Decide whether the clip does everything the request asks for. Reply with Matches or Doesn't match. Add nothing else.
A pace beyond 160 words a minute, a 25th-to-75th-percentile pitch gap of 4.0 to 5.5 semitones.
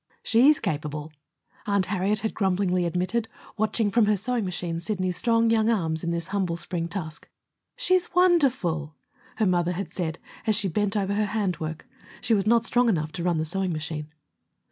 Matches